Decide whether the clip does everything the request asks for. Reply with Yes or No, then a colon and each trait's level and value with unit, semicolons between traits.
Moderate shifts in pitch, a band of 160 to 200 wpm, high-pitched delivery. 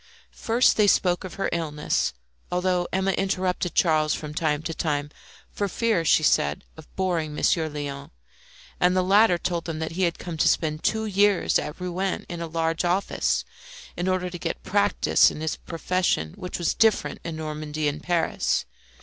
No: average, 3.1 semitones; average, 175 wpm; medium, 175 Hz